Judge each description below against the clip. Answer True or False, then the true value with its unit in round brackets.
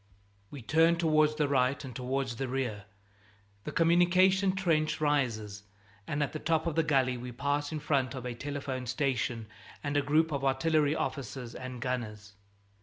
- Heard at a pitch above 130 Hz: True (140 Hz)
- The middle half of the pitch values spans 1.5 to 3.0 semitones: False (3.5 semitones)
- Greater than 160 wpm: True (170 wpm)